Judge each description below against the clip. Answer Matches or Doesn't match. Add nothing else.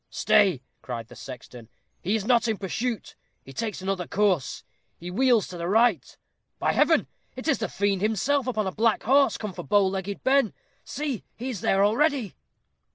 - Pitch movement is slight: Doesn't match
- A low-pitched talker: Doesn't match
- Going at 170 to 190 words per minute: Matches